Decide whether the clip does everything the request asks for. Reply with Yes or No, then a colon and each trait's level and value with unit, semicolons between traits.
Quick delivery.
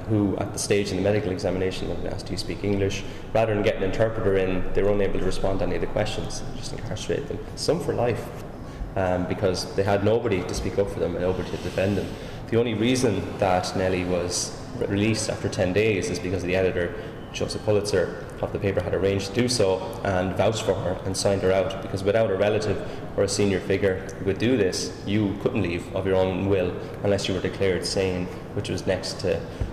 Yes: fast, 230 wpm